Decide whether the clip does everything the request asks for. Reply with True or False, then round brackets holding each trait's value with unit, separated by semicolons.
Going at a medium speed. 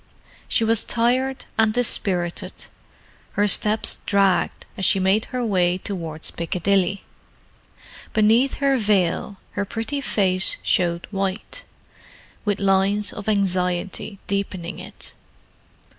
False (110 wpm)